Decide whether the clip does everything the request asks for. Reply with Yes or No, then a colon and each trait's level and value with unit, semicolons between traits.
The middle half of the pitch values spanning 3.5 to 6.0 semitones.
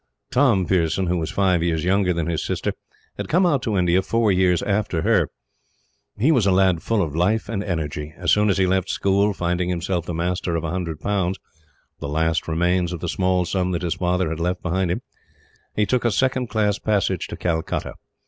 No: average, 2.9 semitones